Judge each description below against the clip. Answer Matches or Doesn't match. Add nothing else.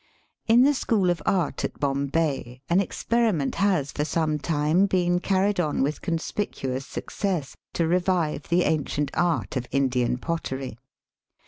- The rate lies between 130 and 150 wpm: Matches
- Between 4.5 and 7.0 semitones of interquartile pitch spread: Matches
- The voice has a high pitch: Doesn't match